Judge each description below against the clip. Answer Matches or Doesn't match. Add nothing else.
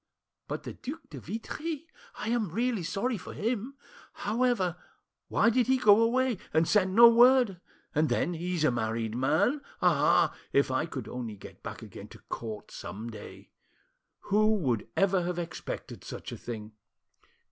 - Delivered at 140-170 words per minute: Matches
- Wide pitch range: Matches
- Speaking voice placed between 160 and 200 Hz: Matches